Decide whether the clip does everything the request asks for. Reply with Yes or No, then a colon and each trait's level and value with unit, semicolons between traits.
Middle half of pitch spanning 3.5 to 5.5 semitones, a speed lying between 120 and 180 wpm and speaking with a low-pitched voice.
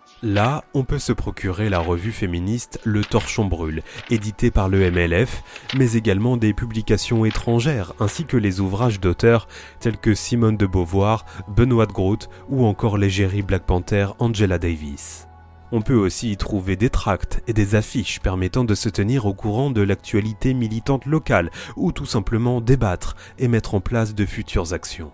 Yes: average, 3.8 semitones; average, 170 wpm; low, 105 Hz